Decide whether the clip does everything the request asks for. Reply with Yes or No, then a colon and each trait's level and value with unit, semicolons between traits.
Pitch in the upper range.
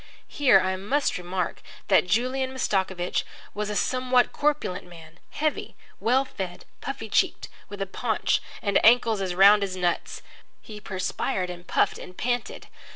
Yes: high, 200 Hz